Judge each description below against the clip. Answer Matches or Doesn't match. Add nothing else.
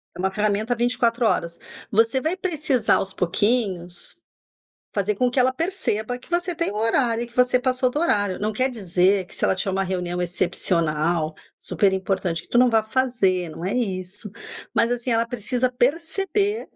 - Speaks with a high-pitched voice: Matches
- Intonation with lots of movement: Doesn't match